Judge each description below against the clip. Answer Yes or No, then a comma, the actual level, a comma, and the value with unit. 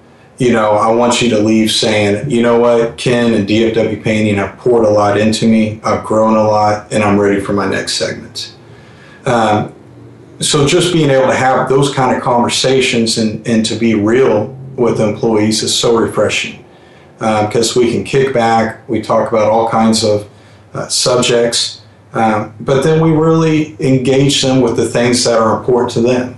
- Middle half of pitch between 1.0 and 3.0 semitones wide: Yes, narrow, 2.6 semitones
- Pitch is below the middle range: Yes, low, 115 Hz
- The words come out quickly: No, average, 185 wpm